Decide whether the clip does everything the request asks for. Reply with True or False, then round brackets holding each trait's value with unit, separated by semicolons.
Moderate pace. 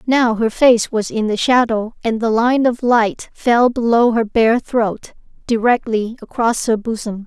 True (175 wpm)